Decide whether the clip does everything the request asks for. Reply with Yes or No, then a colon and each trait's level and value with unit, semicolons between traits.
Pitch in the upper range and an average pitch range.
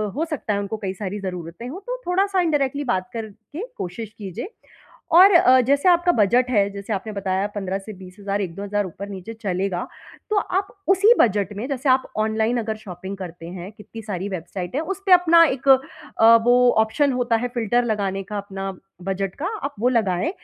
No: high, 220 Hz; wide, 5.8 semitones